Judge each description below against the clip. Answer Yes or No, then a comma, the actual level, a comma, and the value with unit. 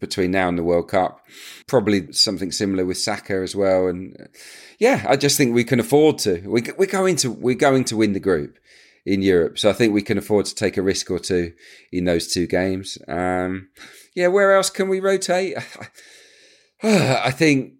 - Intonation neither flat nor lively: No, wide, 8.6 semitones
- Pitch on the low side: Yes, low, 105 Hz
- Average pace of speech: Yes, average, 195 wpm